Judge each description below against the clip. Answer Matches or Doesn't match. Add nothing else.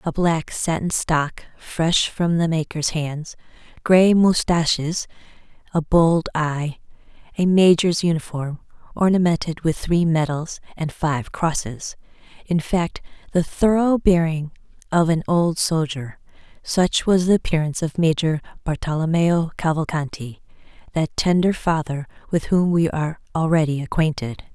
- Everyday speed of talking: Doesn't match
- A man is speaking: Doesn't match